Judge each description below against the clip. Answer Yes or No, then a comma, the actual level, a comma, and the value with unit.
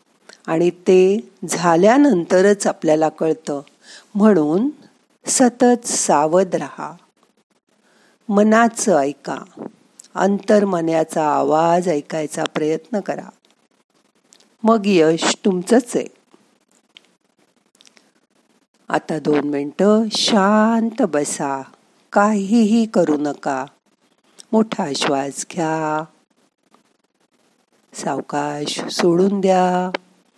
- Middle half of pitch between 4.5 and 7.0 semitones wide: Yes, wide, 5.5 semitones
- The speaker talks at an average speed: No, slow, 70 wpm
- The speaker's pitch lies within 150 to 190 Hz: Yes, medium, 185 Hz